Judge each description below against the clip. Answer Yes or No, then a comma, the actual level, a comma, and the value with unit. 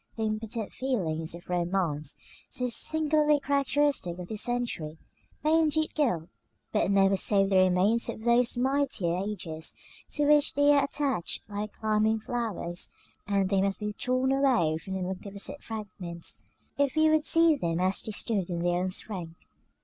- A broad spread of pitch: Yes, wide, 7.0 semitones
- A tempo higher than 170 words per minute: No, average, 160 wpm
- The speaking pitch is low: No, high, 210 Hz